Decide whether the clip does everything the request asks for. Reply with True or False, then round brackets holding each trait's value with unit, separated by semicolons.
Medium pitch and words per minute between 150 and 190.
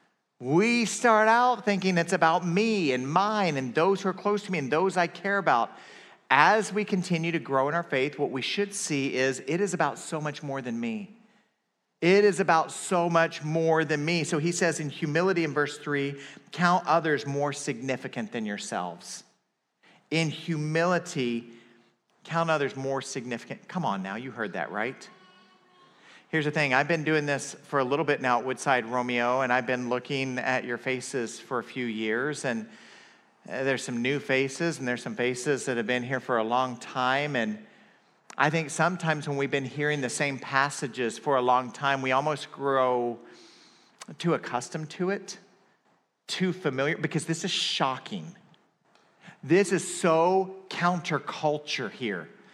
True (150 Hz; 175 wpm)